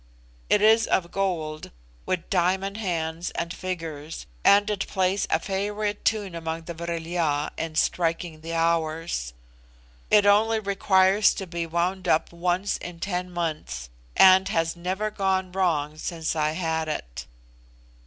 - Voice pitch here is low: No, medium, 175 Hz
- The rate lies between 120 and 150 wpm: Yes, average, 145 wpm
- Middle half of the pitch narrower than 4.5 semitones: Yes, average, 2.9 semitones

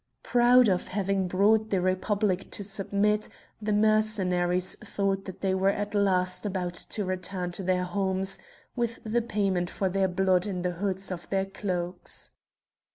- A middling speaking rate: Yes, average, 160 wpm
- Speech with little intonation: Yes, narrow, 2.1 semitones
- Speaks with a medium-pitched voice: No, high, 195 Hz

